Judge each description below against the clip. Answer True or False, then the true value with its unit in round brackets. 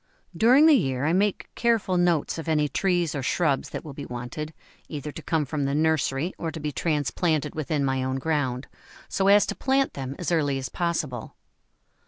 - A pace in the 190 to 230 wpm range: True (195 wpm)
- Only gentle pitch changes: False (4.3 semitones)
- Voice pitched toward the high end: False (155 Hz)